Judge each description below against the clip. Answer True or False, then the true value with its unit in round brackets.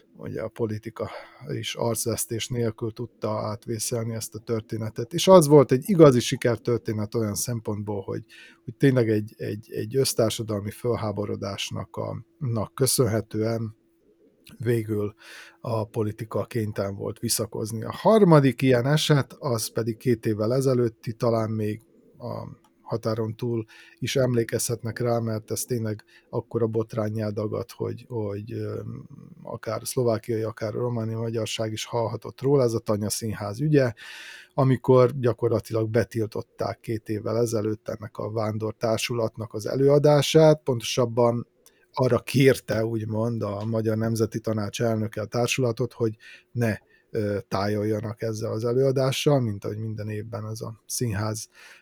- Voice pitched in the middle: False (115 Hz)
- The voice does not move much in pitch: True (1.9 semitones)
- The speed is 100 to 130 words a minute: True (125 wpm)